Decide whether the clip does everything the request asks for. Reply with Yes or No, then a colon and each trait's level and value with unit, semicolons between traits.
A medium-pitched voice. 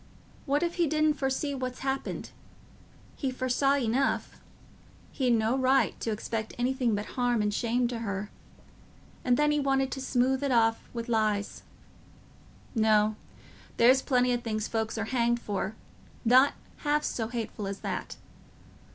No: high, 245 Hz